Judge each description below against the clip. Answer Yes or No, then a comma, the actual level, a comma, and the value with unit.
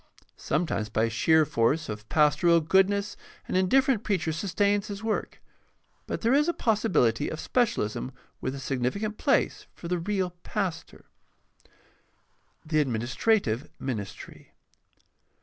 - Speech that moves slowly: Yes, slow, 120 wpm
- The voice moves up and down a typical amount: No, wide, 7.8 semitones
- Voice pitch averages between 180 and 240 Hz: No, medium, 170 Hz